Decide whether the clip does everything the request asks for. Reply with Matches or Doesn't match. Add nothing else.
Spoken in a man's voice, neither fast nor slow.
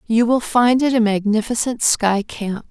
Doesn't match